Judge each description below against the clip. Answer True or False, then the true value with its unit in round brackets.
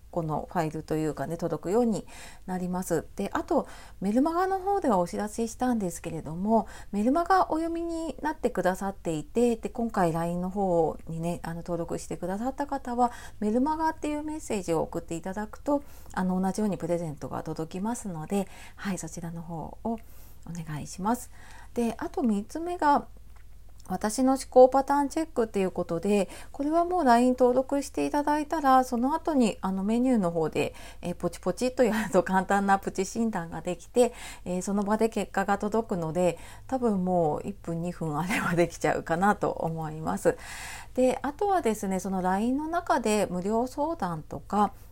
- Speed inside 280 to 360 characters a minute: False (370 characters per minute)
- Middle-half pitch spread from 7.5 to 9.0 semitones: False (6.5 semitones)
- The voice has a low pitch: False (205 Hz)